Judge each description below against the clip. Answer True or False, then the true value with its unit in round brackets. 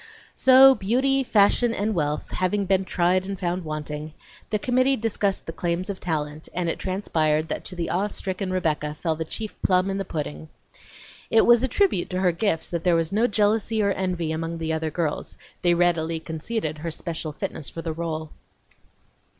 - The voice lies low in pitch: False (180 Hz)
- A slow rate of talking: False (190 wpm)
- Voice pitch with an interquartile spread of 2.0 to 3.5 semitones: False (4.2 semitones)